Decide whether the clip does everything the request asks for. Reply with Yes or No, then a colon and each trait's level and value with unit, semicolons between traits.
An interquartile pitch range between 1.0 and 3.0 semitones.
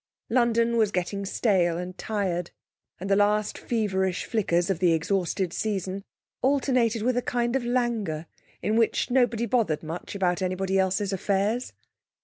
No: average, 4.1 semitones